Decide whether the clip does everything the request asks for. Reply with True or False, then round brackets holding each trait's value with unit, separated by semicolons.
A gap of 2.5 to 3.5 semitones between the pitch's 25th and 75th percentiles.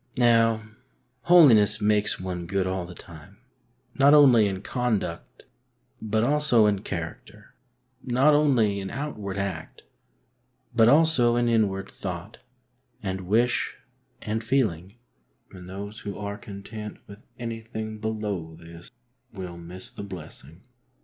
False (3.9 semitones)